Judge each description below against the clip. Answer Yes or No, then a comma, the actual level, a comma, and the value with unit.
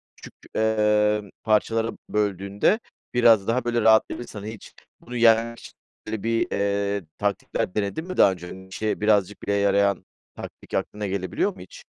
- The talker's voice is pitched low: Yes, low, 105 Hz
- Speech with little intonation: Yes, narrow, 2.1 semitones